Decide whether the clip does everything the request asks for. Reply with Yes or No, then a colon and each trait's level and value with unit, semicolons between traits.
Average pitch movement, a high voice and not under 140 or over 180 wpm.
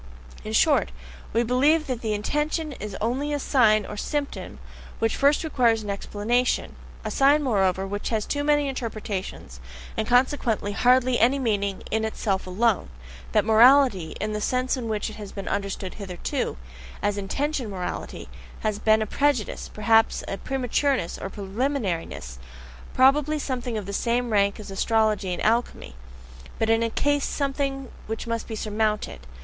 Yes: average, 4.4 semitones; high, 225 Hz; average, 155 wpm